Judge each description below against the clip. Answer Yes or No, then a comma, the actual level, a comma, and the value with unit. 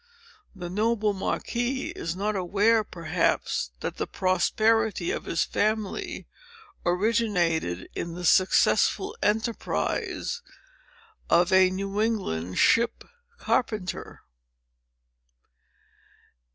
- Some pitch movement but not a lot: Yes, average, 3.9 semitones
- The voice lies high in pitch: Yes, high, 200 Hz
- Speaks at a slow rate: Yes, slow, 85 wpm